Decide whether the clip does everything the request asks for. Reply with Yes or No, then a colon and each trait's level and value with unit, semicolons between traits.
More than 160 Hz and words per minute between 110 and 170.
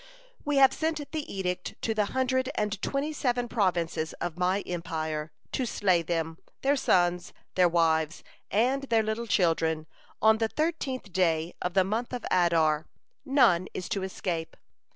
Yes: high, 190 Hz; average, 155 wpm